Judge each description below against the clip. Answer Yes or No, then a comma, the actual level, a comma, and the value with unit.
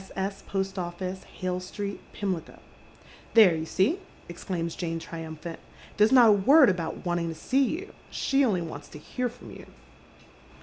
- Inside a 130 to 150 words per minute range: No, average, 170 wpm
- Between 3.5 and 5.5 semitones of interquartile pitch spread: Yes, average, 4.3 semitones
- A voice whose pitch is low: No, medium, 185 Hz